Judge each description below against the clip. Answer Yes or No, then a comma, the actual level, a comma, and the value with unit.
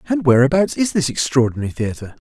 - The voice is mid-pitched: Yes, medium, 145 Hz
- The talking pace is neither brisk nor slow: Yes, average, 160 wpm